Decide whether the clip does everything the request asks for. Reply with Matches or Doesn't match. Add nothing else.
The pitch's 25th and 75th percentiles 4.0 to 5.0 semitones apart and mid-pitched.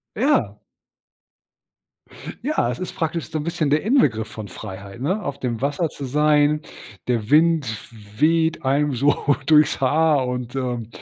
Matches